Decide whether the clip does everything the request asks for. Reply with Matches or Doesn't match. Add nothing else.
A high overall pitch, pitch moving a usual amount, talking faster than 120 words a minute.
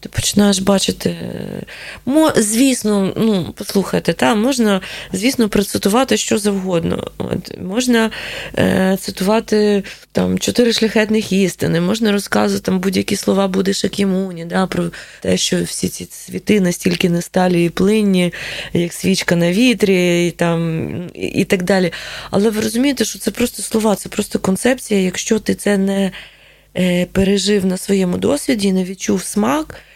Matches